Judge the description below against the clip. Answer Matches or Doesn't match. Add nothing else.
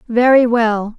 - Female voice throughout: Matches